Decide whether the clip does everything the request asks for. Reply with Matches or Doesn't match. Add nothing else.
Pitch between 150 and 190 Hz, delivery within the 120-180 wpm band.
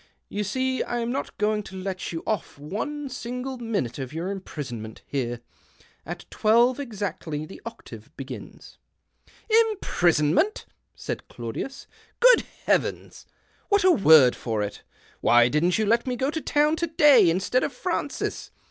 Doesn't match